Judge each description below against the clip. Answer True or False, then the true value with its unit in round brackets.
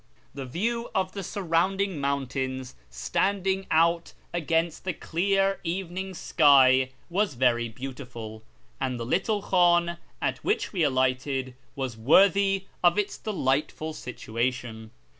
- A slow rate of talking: True (120 wpm)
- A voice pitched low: False (160 Hz)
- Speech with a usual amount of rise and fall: False (6.6 semitones)